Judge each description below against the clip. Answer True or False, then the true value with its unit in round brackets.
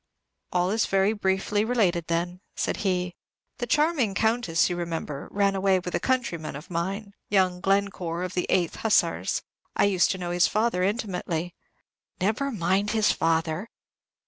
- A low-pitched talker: False (190 Hz)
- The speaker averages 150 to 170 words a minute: True (155 wpm)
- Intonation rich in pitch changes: False (3.1 semitones)